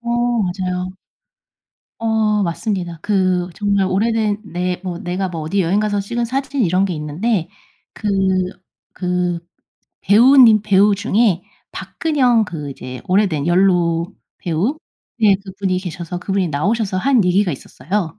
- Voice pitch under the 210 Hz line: Yes, high, 190 Hz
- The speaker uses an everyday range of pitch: Yes, average, 3.2 semitones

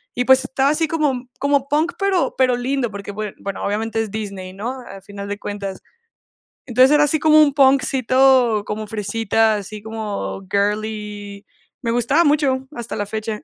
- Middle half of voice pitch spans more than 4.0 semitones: Yes, average, 4.5 semitones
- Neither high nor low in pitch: No, high, 225 Hz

